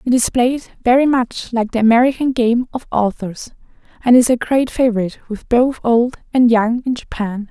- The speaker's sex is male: No, female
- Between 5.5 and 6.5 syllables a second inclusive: No, 5.1 syllables/s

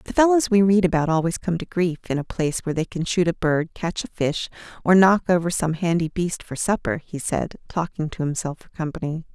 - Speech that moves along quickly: Yes, fast, 230 wpm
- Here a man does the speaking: No, female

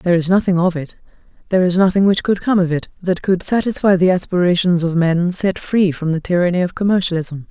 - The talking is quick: Yes, fast, 210 wpm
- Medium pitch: Yes, medium, 180 Hz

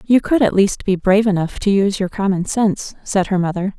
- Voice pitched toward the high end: Yes, high, 195 Hz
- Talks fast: Yes, fast, 240 wpm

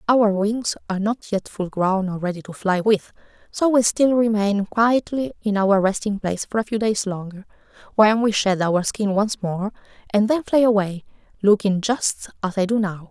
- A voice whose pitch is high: Yes, high, 205 Hz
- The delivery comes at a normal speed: Yes, average, 195 wpm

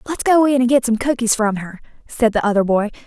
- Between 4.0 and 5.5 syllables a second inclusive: No, 5.9 syllables/s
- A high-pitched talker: Yes, high, 235 Hz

